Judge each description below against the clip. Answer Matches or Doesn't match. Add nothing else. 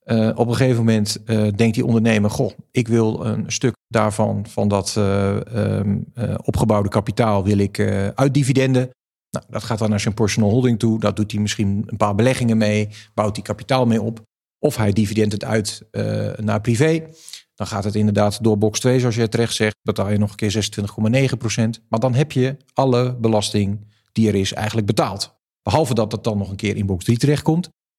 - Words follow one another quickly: Matches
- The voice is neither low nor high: Doesn't match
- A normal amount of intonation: Doesn't match